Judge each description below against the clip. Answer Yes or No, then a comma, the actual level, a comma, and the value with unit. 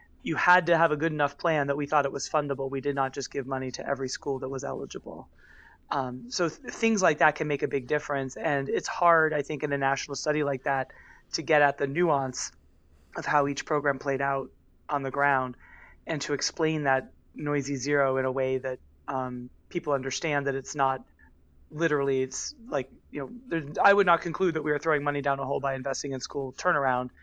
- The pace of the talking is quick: Yes, fast, 220 wpm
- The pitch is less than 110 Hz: No, medium, 140 Hz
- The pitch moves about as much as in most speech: No, narrow, 2.2 semitones